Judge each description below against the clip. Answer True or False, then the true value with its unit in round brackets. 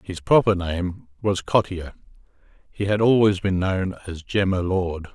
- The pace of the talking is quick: False (150 wpm)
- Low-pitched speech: True (95 Hz)